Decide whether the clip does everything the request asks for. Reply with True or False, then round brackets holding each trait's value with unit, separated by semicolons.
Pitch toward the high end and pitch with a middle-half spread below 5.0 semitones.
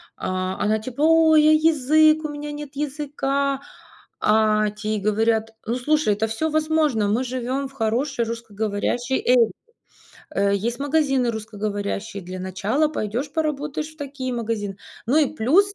False (250 Hz; 5.6 semitones)